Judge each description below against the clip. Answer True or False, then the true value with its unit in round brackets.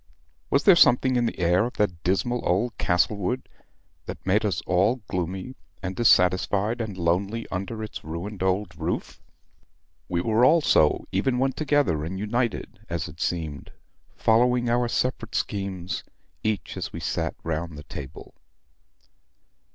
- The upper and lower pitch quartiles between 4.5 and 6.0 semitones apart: True (5.0 semitones)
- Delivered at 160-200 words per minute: False (145 wpm)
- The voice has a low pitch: True (100 Hz)